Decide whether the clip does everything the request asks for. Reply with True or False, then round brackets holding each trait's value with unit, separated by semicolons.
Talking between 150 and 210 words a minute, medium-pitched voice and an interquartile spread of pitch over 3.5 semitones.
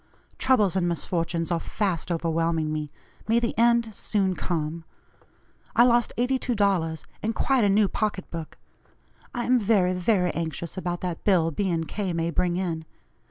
True (160 wpm; 180 Hz; 4.4 semitones)